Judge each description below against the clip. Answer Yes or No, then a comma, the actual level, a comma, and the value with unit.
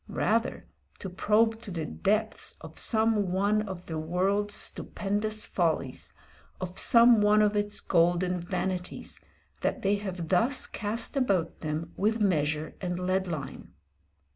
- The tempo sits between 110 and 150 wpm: Yes, average, 140 wpm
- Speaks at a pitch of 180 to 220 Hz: Yes, high, 190 Hz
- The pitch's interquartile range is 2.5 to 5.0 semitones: Yes, average, 3.3 semitones